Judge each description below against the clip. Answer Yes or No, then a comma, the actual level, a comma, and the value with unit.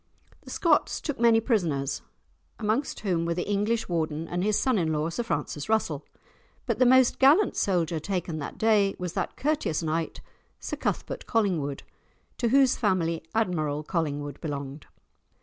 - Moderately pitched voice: Yes, medium, 180 Hz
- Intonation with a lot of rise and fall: Yes, wide, 6.3 semitones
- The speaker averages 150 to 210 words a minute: Yes, average, 155 wpm